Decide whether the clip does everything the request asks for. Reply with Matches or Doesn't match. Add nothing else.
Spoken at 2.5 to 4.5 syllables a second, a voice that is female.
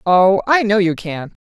Matches